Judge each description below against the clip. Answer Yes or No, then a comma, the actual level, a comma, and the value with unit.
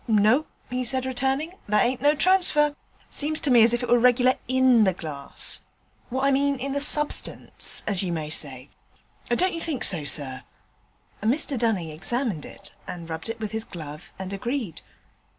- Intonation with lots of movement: Yes, wide, 6.8 semitones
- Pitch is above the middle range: Yes, high, 240 Hz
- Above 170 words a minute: Yes, average, 180 wpm